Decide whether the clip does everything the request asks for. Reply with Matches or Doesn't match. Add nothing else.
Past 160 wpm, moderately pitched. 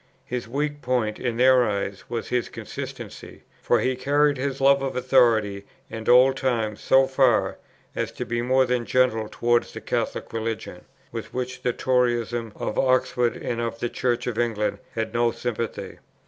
Doesn't match